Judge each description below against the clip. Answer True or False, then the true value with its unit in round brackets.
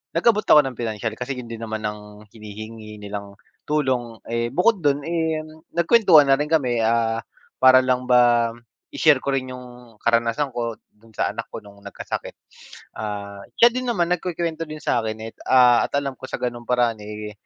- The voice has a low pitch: True (120 Hz)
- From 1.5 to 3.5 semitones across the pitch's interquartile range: False (4.8 semitones)